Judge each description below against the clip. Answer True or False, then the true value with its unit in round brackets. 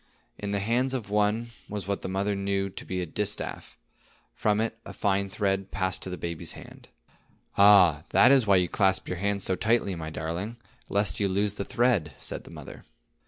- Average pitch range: False (1.9 semitones)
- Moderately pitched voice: False (100 Hz)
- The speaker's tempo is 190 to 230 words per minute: True (200 wpm)